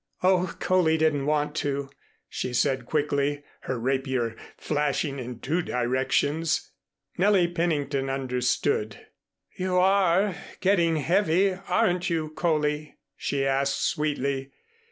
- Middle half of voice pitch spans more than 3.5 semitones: Yes, average, 4.3 semitones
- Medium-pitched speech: Yes, medium, 150 Hz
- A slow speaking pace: Yes, slow, 110 wpm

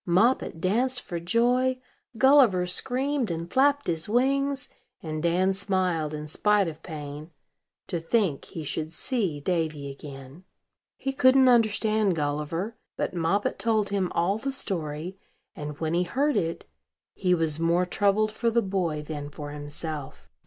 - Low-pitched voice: No, medium, 180 Hz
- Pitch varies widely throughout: Yes, wide, 6.4 semitones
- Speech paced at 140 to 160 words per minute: Yes, average, 145 wpm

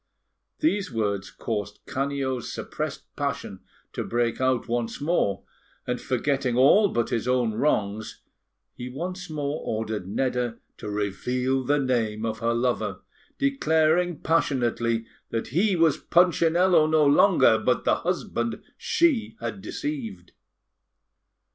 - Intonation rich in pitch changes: Yes, wide, 5.9 semitones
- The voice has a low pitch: Yes, low, 130 Hz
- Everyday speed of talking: No, slow, 125 wpm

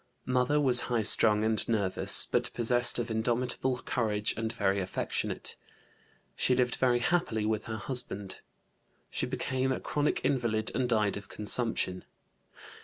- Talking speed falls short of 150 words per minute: Yes, average, 140 wpm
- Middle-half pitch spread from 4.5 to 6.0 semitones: No, average, 2.9 semitones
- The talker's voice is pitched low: Yes, low, 115 Hz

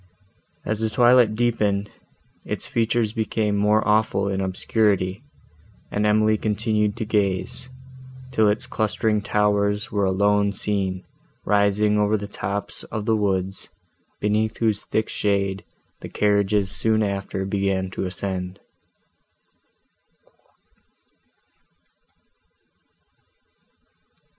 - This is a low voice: Yes, low, 105 Hz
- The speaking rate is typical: No, slow, 100 wpm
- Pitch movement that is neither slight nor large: No, narrow, 1.6 semitones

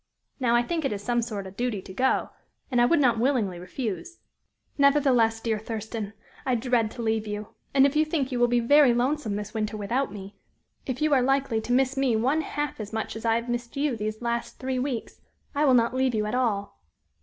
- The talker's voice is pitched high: Yes, high, 240 Hz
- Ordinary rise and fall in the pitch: Yes, average, 3.4 semitones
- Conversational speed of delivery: No, fast, 225 wpm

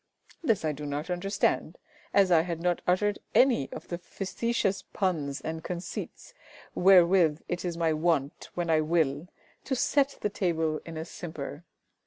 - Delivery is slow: No, average, 160 wpm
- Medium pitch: Yes, medium, 170 Hz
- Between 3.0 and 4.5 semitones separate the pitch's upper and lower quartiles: Yes, average, 3.4 semitones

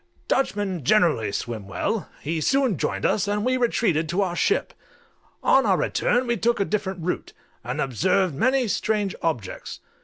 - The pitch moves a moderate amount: No, wide, 6.1 semitones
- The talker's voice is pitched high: Yes, high, 195 Hz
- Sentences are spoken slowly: No, average, 160 wpm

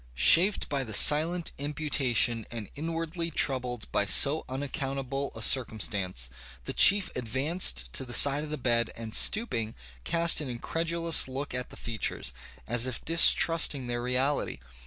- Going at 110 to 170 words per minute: Yes, average, 145 wpm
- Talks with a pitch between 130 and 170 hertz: Yes, low, 135 Hz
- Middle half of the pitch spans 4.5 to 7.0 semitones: Yes, average, 5.1 semitones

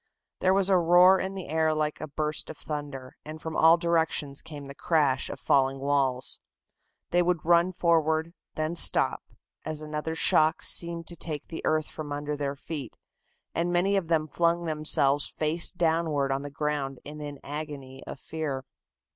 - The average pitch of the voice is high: No, medium, 155 Hz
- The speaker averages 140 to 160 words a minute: No, average, 175 wpm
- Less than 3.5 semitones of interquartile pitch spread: Yes, narrow, 2.6 semitones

